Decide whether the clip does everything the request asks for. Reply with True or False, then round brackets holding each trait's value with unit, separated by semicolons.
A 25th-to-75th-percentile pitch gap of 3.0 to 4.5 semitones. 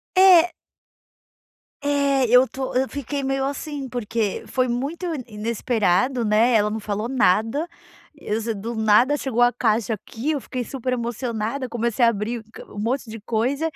True (3.6 semitones)